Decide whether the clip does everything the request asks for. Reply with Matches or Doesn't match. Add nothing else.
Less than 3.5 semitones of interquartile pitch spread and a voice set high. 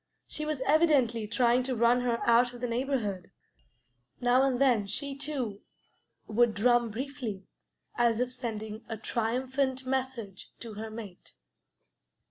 Matches